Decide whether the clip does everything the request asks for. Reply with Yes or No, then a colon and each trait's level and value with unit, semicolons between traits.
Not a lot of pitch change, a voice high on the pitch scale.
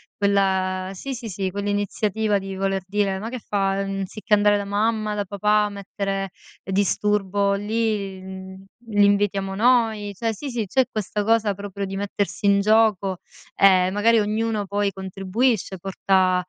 Yes: narrow, 1.5 semitones; high, 200 Hz